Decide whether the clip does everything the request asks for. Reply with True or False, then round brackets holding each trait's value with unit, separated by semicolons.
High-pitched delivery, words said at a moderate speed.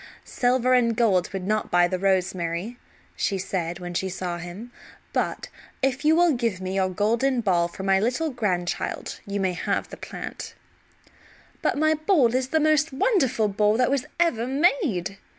True (220 Hz; 170 wpm)